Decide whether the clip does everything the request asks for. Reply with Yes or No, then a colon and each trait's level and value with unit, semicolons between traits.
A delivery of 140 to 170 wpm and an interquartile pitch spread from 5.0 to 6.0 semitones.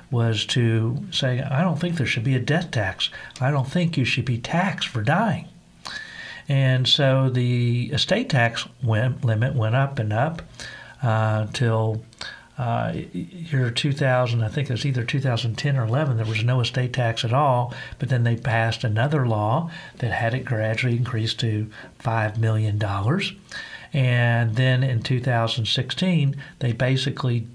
No: average, 155 wpm; average, 3.5 semitones